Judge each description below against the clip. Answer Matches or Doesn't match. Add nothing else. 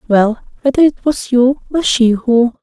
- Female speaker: Matches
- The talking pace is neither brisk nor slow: Matches